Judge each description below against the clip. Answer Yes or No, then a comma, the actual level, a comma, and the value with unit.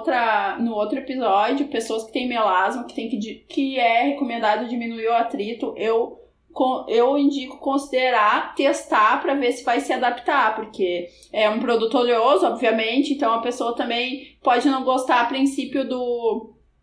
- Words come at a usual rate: Yes, average, 150 wpm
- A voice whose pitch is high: Yes, high, 245 Hz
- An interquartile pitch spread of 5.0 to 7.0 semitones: No, average, 3.3 semitones